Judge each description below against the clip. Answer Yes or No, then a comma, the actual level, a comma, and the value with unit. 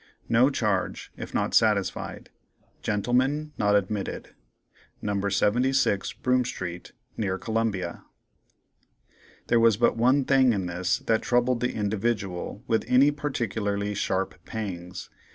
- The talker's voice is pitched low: Yes, low, 110 Hz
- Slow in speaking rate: Yes, slow, 115 wpm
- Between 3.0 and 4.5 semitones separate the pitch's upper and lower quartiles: Yes, average, 4.0 semitones